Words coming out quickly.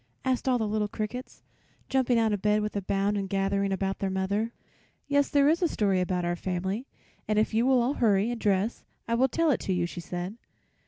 Yes: fast, 225 wpm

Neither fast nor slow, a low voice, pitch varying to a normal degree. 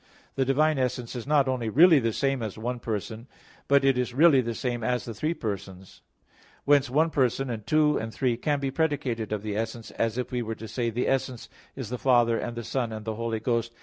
No: fast, 230 wpm; low, 120 Hz; average, 3.2 semitones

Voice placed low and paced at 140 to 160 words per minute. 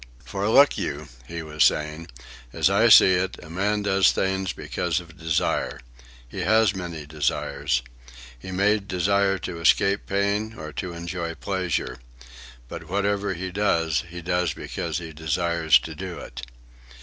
Yes: very low, 90 Hz; average, 150 wpm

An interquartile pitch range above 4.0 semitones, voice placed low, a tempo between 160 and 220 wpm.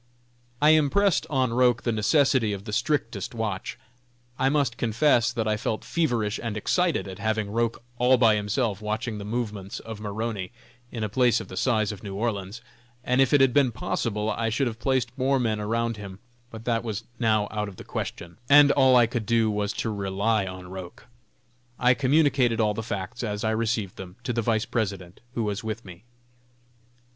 No: average, 3.0 semitones; low, 115 Hz; average, 195 wpm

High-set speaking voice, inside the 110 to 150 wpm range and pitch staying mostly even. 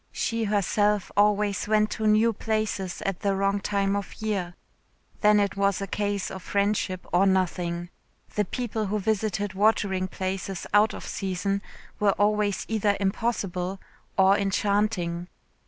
Yes: high, 200 Hz; average, 140 wpm; narrow, 1.7 semitones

